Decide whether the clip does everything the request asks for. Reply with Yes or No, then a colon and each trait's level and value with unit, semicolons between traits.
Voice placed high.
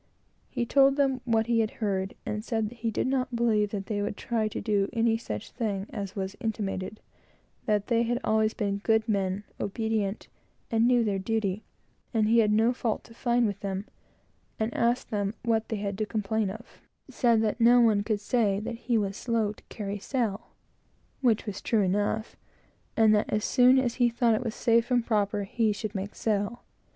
Yes: high, 220 Hz